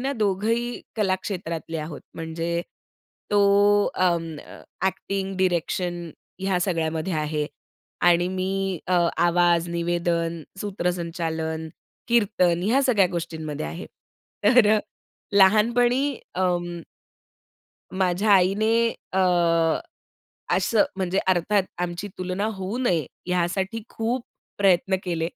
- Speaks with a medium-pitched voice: Yes, medium, 180 Hz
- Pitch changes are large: No, average, 2.9 semitones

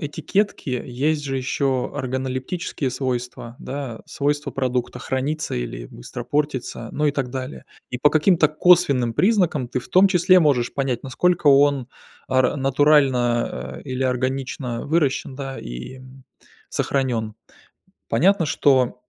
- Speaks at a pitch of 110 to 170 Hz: Yes, low, 135 Hz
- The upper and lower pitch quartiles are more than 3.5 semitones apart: No, average, 2.9 semitones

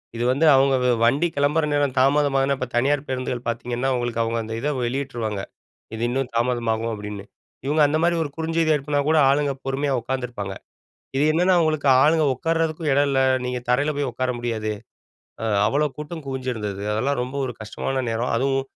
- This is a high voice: No, low, 135 Hz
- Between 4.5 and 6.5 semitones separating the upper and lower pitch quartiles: No, average, 3.4 semitones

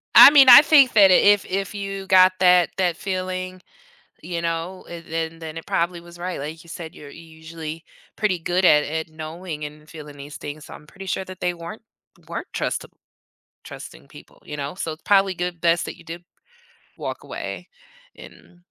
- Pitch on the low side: No, medium, 175 Hz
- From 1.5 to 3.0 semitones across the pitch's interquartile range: Yes, narrow, 2.6 semitones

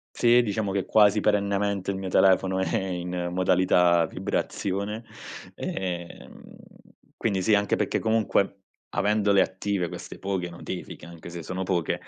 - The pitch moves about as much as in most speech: No, narrow, 2.2 semitones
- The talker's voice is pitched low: Yes, very low, 95 Hz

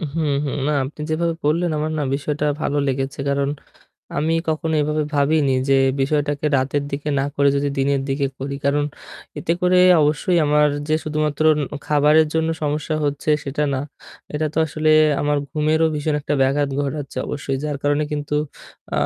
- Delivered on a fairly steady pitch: Yes, narrow, 1.6 semitones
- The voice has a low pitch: No, medium, 150 Hz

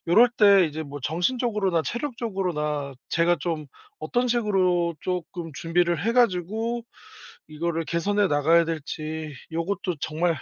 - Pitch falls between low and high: Yes, medium, 175 Hz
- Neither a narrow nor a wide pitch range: Yes, average, 4.4 semitones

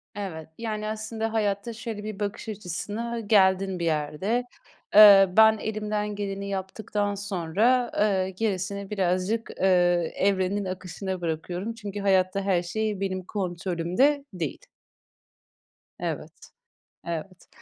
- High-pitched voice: Yes, high, 200 Hz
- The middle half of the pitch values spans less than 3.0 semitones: Yes, narrow, 2.6 semitones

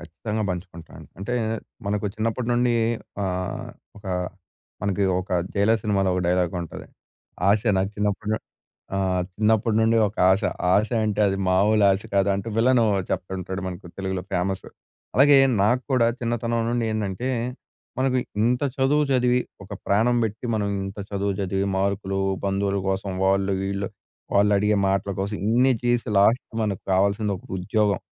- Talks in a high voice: No, low, 100 Hz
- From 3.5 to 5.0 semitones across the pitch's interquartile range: No, average, 2.7 semitones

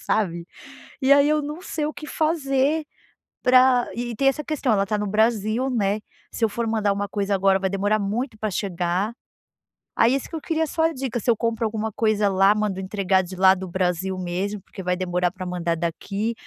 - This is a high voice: Yes, high, 210 Hz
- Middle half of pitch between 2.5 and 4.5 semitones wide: No, average, 4.9 semitones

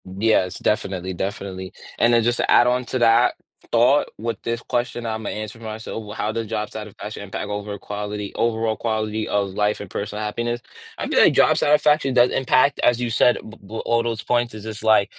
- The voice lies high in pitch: No, low, 110 Hz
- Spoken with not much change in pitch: Yes, narrow, 2.3 semitones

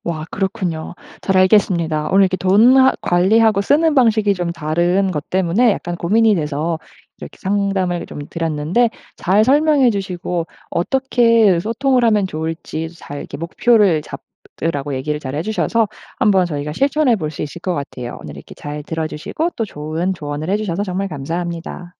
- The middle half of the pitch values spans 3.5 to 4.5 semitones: No, average, 5.2 semitones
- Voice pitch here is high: No, medium, 180 Hz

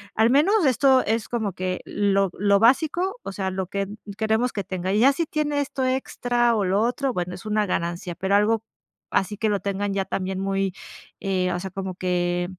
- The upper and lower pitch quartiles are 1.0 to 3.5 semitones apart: No, average, 4.3 semitones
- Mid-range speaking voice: No, high, 205 Hz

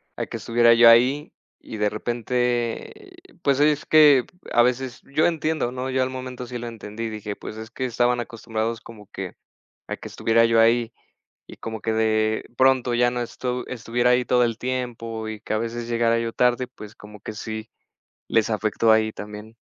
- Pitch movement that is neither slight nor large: No, narrow, 2.2 semitones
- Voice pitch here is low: Yes, low, 115 Hz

